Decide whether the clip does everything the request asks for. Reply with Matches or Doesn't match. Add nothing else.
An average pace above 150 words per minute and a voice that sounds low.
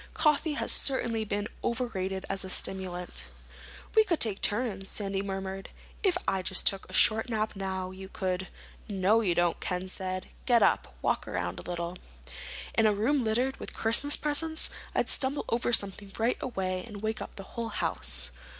Doesn't match